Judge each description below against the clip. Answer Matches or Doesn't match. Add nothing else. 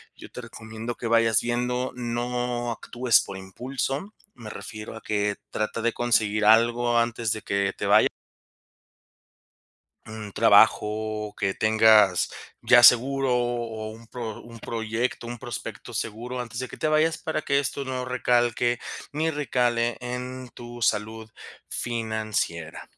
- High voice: Doesn't match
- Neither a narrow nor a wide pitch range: Doesn't match